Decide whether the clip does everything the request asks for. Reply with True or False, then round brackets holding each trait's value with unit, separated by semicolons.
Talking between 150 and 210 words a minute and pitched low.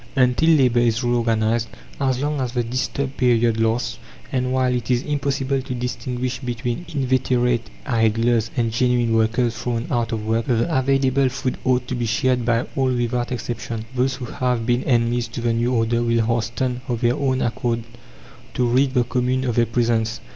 True (180 wpm; 120 Hz)